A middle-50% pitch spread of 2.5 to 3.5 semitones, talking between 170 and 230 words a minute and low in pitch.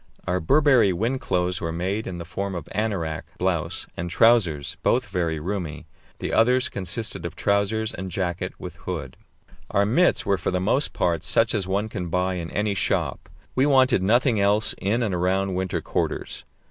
No: average, 3.9 semitones; average, 180 wpm; very low, 95 Hz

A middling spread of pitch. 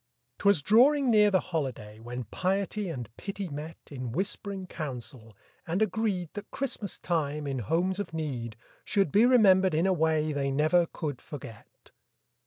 No: wide, 6.3 semitones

